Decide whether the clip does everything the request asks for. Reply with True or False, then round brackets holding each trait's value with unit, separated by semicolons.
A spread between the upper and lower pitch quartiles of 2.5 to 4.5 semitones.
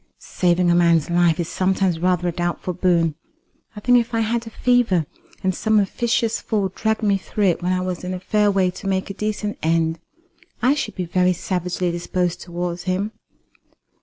True (3.1 semitones)